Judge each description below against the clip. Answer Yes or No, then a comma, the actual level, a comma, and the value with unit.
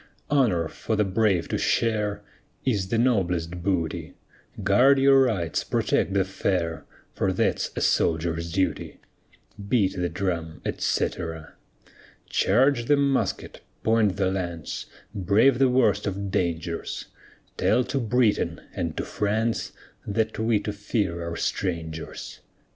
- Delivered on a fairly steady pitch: No, average, 4.7 semitones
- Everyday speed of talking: No, slow, 125 wpm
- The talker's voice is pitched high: No, low, 100 Hz